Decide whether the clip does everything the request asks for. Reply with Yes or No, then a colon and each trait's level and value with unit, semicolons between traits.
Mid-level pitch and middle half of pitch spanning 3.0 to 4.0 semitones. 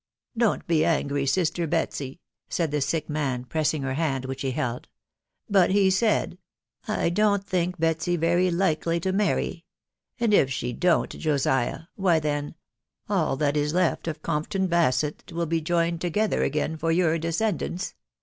Yes: medium, 165 Hz; average, 3.4 semitones